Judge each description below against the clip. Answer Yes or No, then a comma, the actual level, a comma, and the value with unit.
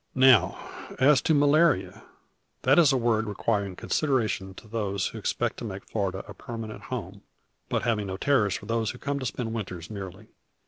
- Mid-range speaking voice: No, low, 110 Hz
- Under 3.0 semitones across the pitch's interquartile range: No, average, 4.6 semitones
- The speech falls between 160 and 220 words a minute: Yes, average, 180 wpm